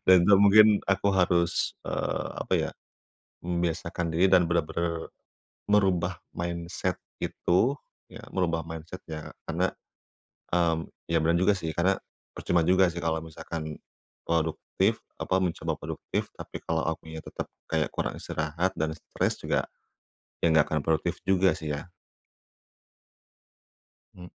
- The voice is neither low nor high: No, very low, 85 Hz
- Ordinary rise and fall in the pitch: No, narrow, 2.1 semitones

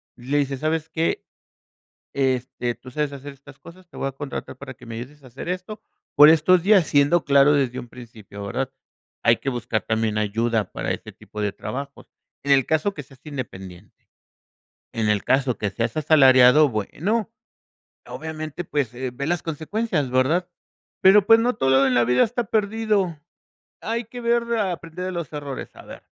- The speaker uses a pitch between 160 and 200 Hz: No, medium, 140 Hz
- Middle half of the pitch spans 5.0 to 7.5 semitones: Yes, wide, 5.5 semitones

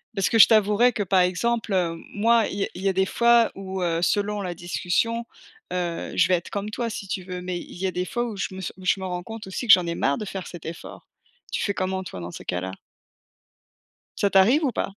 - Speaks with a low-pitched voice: No, high, 190 Hz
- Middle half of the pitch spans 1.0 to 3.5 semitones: Yes, average, 3.1 semitones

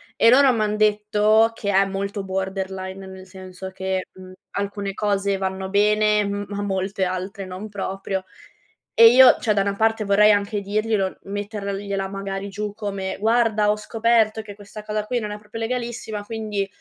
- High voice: Yes, high, 205 Hz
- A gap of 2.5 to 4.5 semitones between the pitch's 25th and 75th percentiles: No, narrow, 1.7 semitones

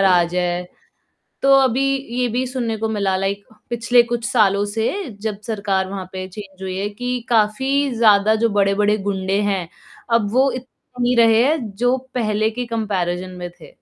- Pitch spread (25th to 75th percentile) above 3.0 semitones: Yes, average, 3.5 semitones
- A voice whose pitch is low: No, high, 210 Hz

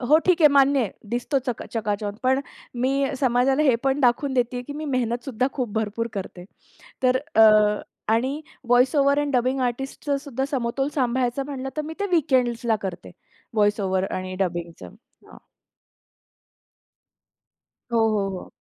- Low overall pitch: No, very high, 250 Hz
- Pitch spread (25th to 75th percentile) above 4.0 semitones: No, average, 3.5 semitones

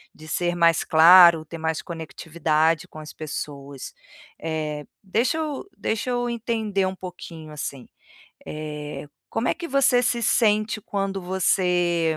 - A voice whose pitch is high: No, medium, 170 Hz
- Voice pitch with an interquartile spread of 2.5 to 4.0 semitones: No, average, 5.3 semitones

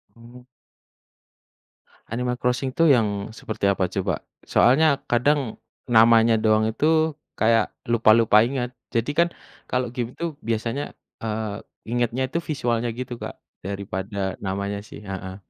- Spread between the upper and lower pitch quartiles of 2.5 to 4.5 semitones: Yes, average, 2.9 semitones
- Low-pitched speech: Yes, low, 115 Hz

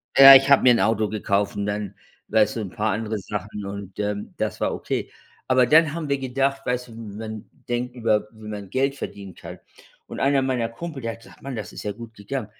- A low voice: Yes, low, 115 Hz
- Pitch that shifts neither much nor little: Yes, average, 4.1 semitones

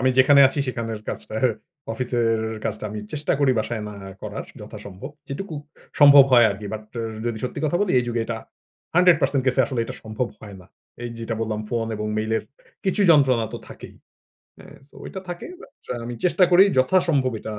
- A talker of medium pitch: No, low, 120 Hz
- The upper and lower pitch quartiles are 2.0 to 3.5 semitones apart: No, average, 4.4 semitones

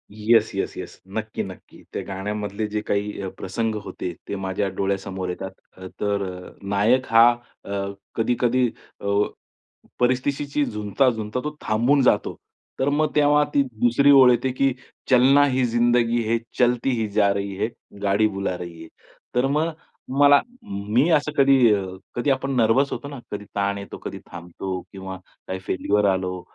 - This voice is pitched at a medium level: No, low, 110 Hz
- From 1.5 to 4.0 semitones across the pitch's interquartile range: No, average, 4.7 semitones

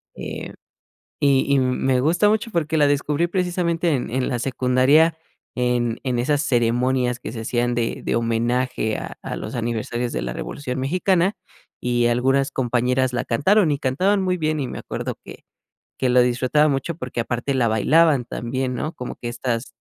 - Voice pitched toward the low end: Yes, low, 130 Hz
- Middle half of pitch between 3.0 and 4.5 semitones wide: Yes, average, 3.8 semitones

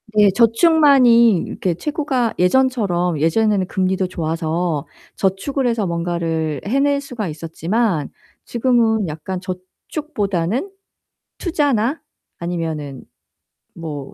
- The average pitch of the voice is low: No, high, 195 Hz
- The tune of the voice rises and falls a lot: Yes, wide, 6.4 semitones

